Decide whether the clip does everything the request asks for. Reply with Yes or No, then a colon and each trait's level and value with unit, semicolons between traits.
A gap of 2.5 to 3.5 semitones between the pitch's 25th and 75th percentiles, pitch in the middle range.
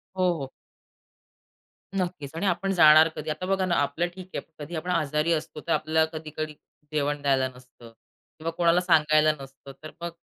Yes: average, 2.8 semitones; medium, 155 Hz